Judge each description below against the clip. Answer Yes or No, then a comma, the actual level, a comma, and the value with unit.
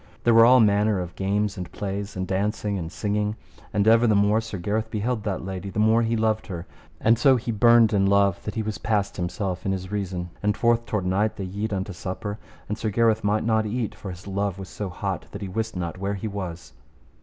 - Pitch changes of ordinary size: No, narrow, 2.3 semitones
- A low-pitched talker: Yes, low, 105 Hz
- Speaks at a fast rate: Yes, fast, 235 wpm